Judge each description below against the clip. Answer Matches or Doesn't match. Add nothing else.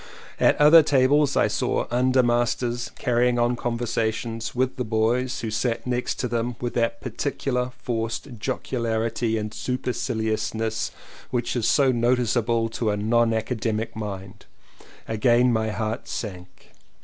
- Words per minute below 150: Matches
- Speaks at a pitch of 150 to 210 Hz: Doesn't match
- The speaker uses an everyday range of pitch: Doesn't match